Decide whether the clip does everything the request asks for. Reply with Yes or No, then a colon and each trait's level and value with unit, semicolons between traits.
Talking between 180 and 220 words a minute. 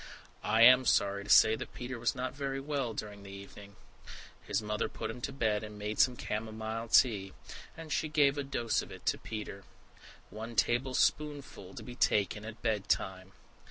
Yes: average, 190 wpm